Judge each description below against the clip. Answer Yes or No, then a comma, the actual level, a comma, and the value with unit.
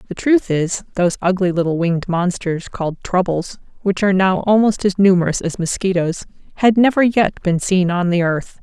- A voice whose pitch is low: No, medium, 185 Hz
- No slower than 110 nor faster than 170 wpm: No, average, 180 wpm